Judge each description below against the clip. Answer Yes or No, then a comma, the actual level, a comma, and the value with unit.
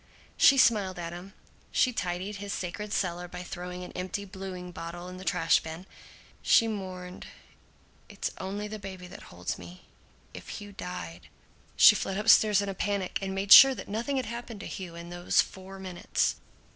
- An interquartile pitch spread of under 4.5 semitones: Yes, narrow, 2.4 semitones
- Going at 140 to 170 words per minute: No, average, 180 wpm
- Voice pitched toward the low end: No, high, 190 Hz